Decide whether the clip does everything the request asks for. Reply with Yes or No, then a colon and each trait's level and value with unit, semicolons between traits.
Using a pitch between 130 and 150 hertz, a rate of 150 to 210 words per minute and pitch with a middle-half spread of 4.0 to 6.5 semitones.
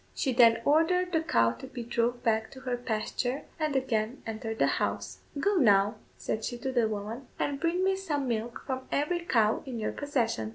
No: high, 245 Hz; average, 200 wpm; average, 4.6 semitones